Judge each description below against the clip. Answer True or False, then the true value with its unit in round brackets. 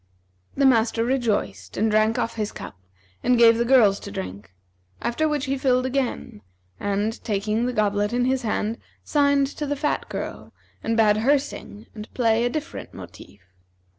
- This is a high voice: True (230 Hz)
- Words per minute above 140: True (170 wpm)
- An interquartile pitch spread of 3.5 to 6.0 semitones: True (3.8 semitones)